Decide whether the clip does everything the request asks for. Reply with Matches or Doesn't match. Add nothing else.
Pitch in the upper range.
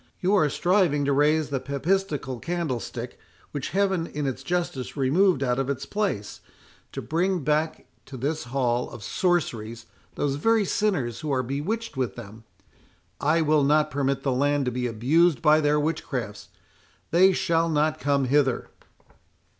Doesn't match